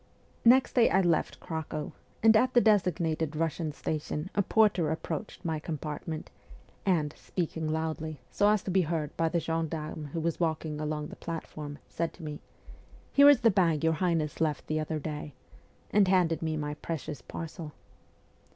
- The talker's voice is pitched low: No, medium, 160 Hz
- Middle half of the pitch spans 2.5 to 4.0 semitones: Yes, average, 2.8 semitones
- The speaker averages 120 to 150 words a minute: No, average, 170 wpm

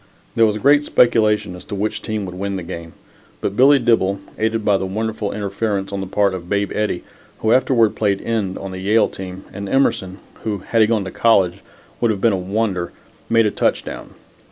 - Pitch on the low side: Yes, low, 105 Hz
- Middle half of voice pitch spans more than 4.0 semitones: No, average, 2.7 semitones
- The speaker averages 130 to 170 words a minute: No, fast, 205 wpm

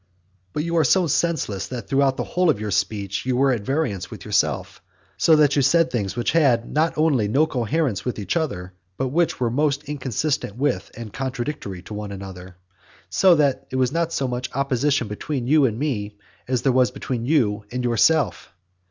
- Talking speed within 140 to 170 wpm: No, average, 200 wpm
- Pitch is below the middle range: Yes, low, 130 Hz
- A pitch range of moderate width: No, wide, 5.9 semitones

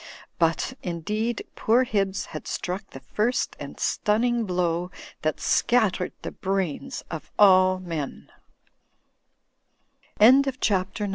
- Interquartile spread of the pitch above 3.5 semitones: Yes, average, 4.0 semitones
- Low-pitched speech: No, high, 190 Hz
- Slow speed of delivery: Yes, slow, 95 wpm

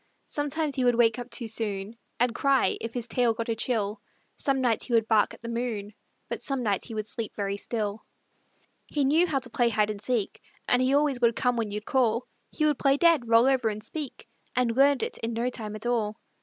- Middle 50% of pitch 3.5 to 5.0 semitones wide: No, average, 3.1 semitones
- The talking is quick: Yes, fast, 230 wpm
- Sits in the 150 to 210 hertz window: No, high, 235 Hz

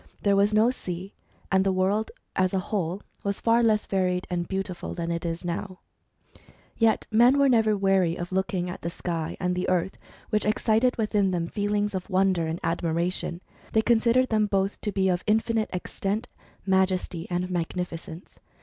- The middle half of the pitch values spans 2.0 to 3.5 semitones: Yes, average, 3.0 semitones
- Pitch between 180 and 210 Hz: Yes, high, 190 Hz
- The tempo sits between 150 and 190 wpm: Yes, average, 175 wpm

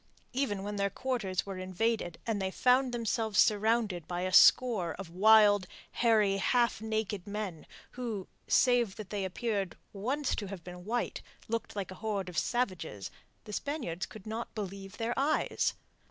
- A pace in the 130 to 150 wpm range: No, average, 160 wpm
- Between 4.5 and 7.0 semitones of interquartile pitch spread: No, average, 3.5 semitones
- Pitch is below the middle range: No, high, 210 Hz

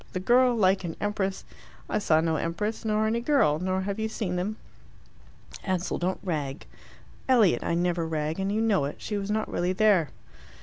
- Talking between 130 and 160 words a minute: No, average, 190 wpm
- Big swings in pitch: No, average, 4.1 semitones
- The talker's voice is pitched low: No, high, 190 Hz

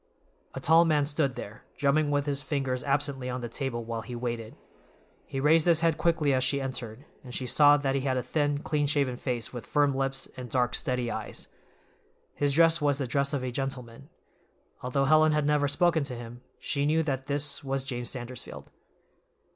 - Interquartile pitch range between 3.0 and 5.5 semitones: No, narrow, 2.6 semitones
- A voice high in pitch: No, medium, 140 Hz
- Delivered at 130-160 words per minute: No, average, 195 wpm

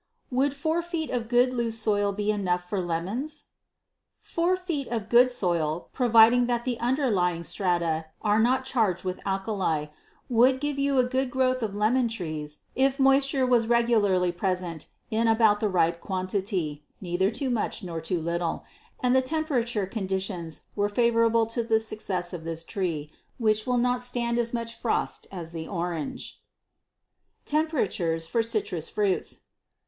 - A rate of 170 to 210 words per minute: No, average, 155 wpm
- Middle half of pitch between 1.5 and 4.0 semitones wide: No, wide, 5.5 semitones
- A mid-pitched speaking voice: No, high, 220 Hz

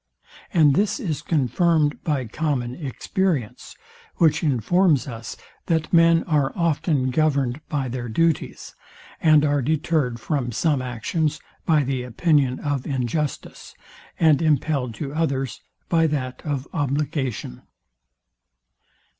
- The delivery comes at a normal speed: No, slow, 115 wpm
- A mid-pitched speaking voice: Yes, medium, 145 Hz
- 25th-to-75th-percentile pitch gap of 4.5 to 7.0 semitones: No, average, 3.8 semitones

